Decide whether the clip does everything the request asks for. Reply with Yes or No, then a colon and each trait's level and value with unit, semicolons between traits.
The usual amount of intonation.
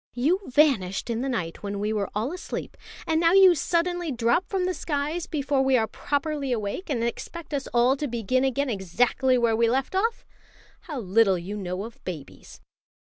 No: wide, 5.8 semitones